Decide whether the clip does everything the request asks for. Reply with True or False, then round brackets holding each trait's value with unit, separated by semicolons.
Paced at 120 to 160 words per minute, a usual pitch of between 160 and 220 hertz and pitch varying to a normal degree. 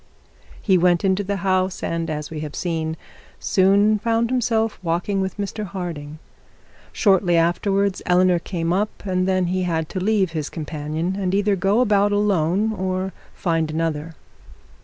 True (155 wpm; 185 Hz; 3.3 semitones)